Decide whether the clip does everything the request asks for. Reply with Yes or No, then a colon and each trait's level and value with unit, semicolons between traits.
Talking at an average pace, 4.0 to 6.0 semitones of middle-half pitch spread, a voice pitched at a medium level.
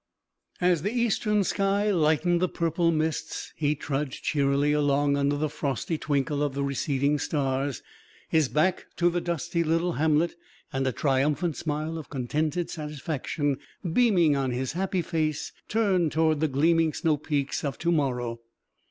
No: average, 150 wpm; average, 3.2 semitones; medium, 155 Hz